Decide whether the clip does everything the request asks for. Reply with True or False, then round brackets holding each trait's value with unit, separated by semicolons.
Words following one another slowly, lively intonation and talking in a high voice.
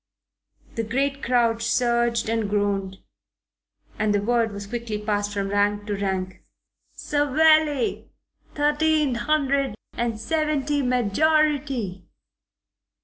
True (100 wpm; 5.7 semitones; 235 Hz)